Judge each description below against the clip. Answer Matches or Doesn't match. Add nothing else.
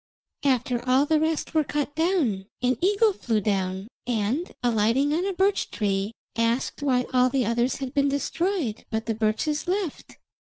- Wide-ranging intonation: Matches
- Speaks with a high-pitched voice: Matches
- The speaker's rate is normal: Matches